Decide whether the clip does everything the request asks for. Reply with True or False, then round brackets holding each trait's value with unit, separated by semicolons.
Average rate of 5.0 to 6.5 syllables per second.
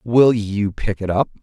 False (3.9 syllables/s)